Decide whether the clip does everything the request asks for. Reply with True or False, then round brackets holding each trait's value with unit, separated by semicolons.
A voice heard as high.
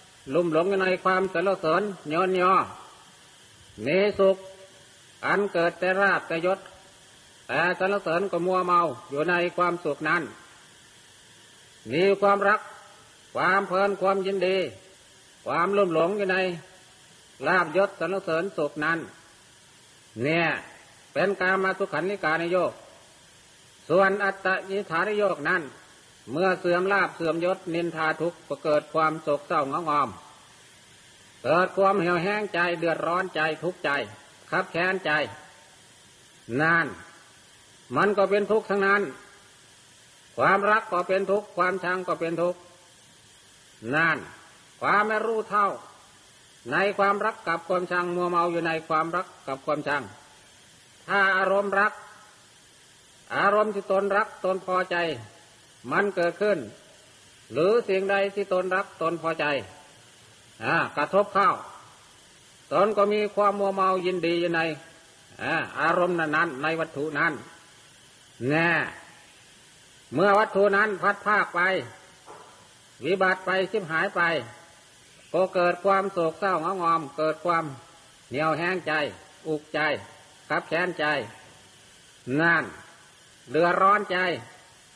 False (180 Hz)